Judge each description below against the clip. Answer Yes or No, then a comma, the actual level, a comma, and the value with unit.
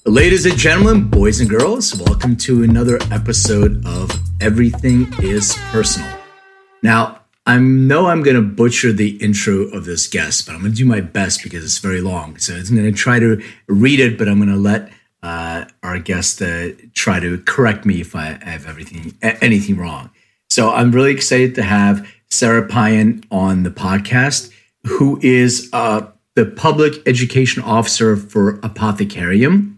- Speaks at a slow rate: No, average, 170 wpm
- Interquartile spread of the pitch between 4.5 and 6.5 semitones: No, average, 3.9 semitones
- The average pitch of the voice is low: Yes, low, 110 Hz